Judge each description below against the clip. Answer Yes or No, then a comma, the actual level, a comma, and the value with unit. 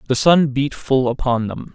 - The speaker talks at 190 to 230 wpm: Yes, fast, 205 wpm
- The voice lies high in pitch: No, low, 135 Hz